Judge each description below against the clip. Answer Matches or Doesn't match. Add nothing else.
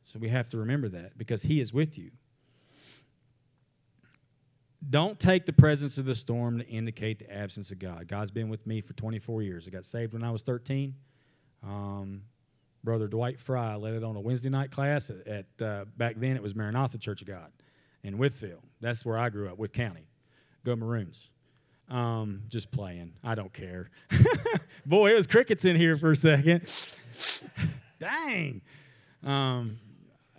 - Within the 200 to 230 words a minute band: Doesn't match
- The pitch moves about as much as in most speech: Matches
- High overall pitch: Doesn't match